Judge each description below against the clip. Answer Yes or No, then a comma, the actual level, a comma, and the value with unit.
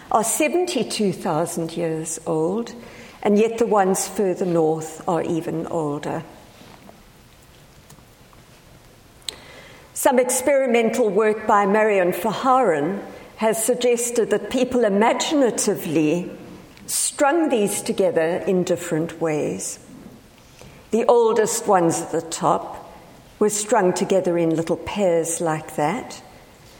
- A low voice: No, high, 195 Hz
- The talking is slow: Yes, slow, 100 wpm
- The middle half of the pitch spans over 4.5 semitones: Yes, wide, 5.6 semitones